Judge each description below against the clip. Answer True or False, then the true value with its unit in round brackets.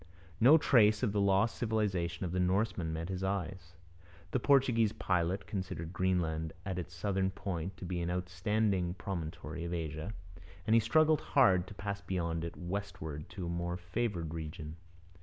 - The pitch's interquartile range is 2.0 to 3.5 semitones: True (3.2 semitones)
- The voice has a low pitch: True (90 Hz)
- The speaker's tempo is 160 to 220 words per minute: True (165 wpm)